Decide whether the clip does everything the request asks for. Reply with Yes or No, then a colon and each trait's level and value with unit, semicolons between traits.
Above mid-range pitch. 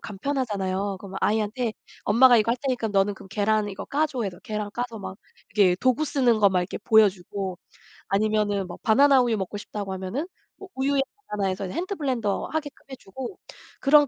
Yes: high, 215 Hz